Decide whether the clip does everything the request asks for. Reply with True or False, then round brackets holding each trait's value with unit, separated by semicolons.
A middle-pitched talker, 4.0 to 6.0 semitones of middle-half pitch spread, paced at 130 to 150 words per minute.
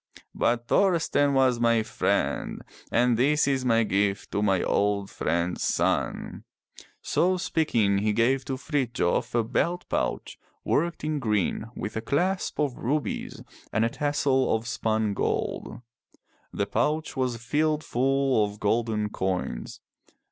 False (120 Hz; 5.0 semitones; 140 wpm)